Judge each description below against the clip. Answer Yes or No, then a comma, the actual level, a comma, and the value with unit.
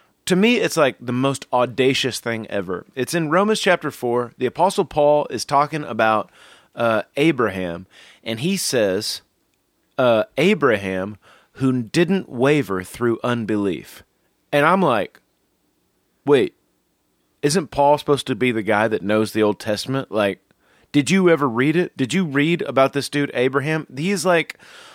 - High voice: No, low, 135 Hz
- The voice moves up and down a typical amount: No, wide, 5.7 semitones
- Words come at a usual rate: Yes, average, 150 wpm